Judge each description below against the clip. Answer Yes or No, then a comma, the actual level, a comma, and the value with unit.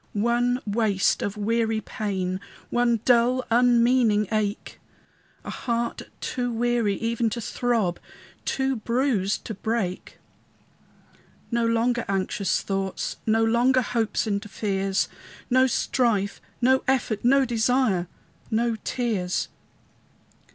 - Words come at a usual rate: No, slow, 110 wpm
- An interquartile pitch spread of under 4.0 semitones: Yes, average, 3.0 semitones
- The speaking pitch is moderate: No, high, 230 Hz